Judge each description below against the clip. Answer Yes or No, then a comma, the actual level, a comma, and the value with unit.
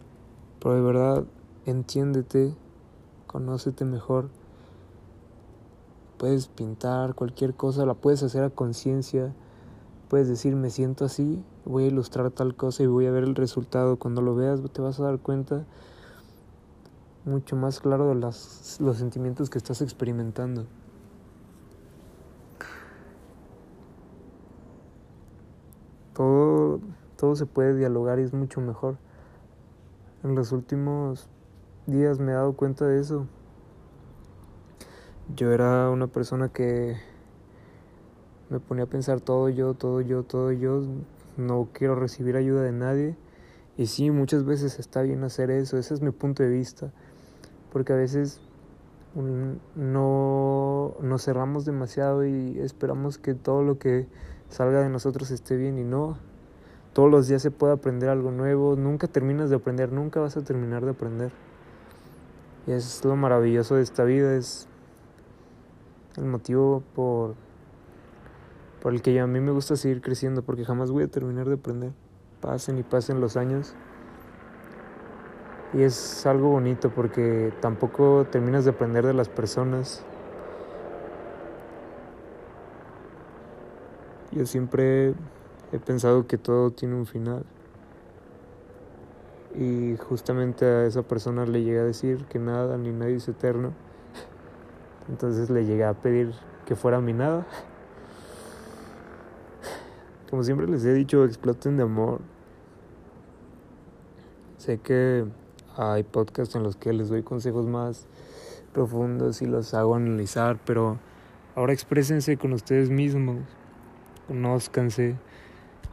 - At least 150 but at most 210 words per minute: No, average, 130 wpm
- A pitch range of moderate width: No, narrow, 2.2 semitones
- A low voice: Yes, low, 130 Hz